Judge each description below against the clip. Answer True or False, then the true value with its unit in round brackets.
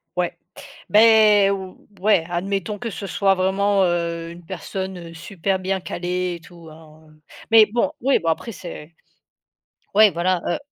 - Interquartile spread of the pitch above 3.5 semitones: False (2.9 semitones)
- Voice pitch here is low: False (185 Hz)